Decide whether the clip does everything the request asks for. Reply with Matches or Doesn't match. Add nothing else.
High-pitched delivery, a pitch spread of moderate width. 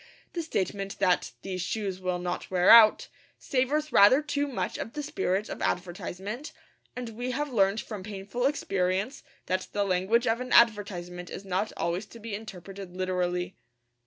Matches